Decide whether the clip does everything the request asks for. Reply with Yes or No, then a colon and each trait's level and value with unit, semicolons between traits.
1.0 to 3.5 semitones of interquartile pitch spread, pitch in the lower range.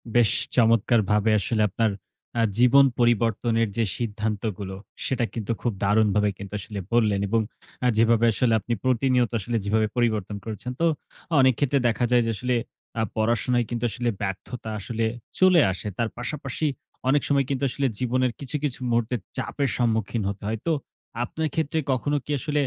Yes: average, 2.7 semitones; low, 115 Hz